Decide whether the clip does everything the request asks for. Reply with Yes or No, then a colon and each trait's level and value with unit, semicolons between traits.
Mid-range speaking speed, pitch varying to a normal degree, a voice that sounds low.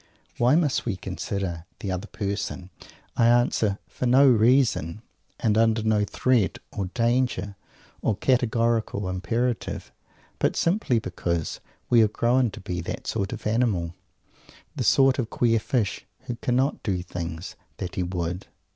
Yes: average, 145 wpm; average, 4.5 semitones; low, 110 Hz